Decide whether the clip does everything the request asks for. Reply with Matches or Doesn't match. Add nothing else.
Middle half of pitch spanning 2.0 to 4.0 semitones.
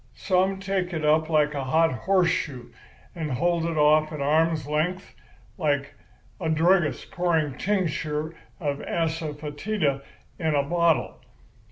Matches